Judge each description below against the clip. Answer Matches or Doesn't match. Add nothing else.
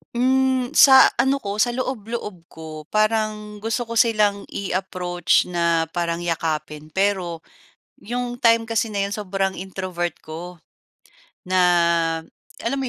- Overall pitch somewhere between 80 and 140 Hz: Doesn't match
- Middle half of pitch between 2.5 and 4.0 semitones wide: Doesn't match